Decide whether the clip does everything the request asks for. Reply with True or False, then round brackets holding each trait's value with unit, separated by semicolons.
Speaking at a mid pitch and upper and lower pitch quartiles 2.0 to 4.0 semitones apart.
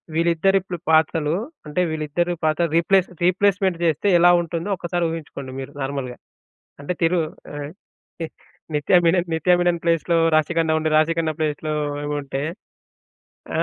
True (165 Hz; 2.4 semitones)